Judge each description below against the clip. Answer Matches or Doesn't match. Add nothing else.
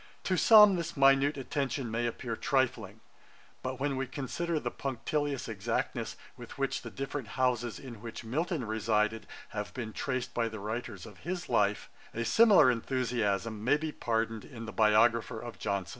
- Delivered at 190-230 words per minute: Doesn't match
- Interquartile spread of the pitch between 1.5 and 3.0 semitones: Doesn't match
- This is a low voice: Matches